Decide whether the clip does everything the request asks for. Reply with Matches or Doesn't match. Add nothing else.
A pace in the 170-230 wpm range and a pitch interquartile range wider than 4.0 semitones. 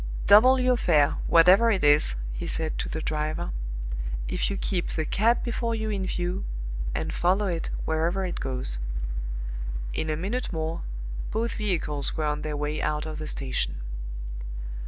Doesn't match